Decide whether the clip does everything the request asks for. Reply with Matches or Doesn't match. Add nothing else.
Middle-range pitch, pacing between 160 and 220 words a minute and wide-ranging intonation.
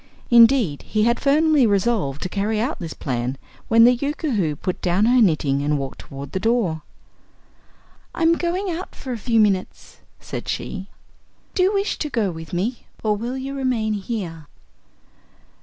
Doesn't match